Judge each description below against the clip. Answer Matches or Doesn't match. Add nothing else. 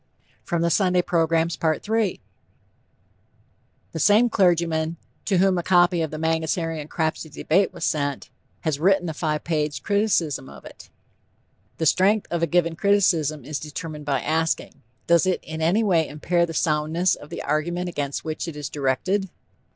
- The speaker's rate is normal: Matches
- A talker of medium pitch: Matches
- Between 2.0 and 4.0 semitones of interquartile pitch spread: Matches